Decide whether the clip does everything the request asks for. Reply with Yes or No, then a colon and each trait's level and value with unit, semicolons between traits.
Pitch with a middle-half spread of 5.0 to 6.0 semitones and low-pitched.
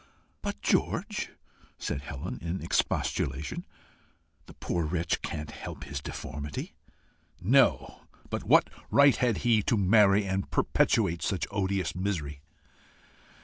Yes: wide, 5.4 semitones; very low, 90 Hz